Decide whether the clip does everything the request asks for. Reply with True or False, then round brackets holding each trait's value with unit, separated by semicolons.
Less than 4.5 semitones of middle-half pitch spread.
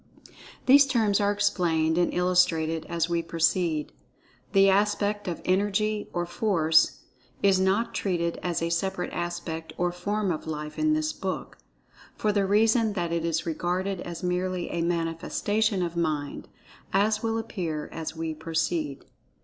True (3.7 semitones)